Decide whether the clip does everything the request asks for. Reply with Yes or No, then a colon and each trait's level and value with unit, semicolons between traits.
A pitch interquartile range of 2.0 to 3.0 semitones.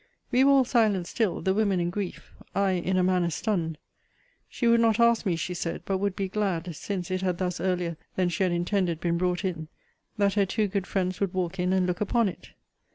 Yes: narrow, 2.4 semitones